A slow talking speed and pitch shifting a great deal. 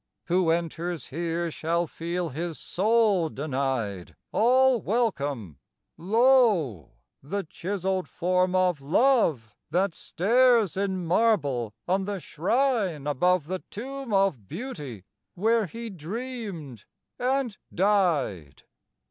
Yes: slow, 105 wpm; wide, 6.3 semitones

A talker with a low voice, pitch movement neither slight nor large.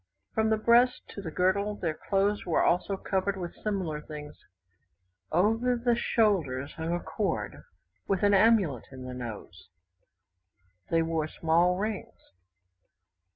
No: medium, 185 Hz; average, 4.7 semitones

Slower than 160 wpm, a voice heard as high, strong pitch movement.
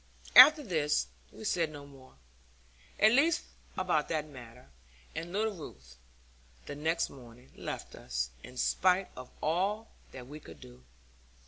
No: average, 140 wpm; medium, 155 Hz; wide, 6.7 semitones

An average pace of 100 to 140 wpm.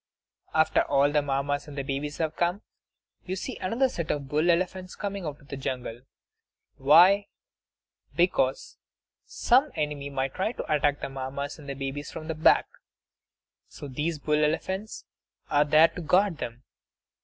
No: average, 155 wpm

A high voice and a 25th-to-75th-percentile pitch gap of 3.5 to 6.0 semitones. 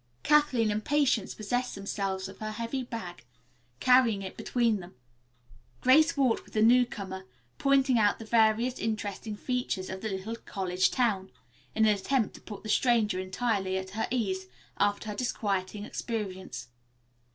Yes: high, 215 Hz; average, 4.1 semitones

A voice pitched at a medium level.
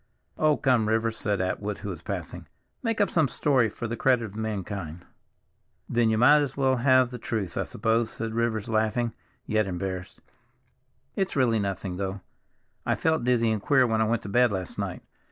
No: low, 115 Hz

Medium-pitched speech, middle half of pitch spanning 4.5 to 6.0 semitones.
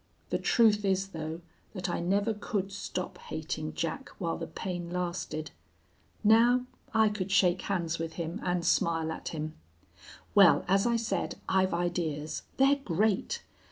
No: medium, 180 Hz; average, 3.7 semitones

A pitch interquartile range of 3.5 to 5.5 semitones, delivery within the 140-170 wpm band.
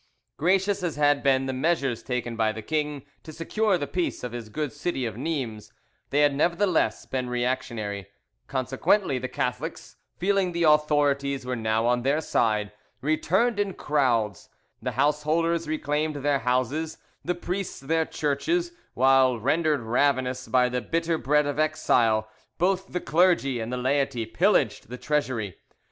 Yes: average, 4.5 semitones; average, 155 wpm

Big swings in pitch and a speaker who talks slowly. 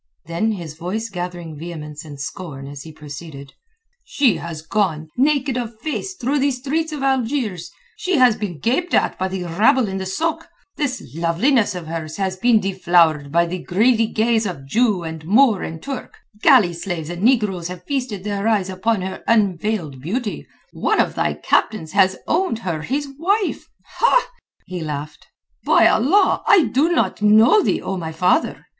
No: wide, 6.8 semitones; average, 170 wpm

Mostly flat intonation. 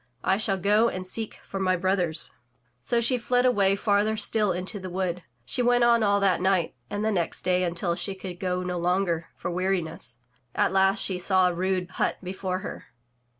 Yes: narrow, 2.2 semitones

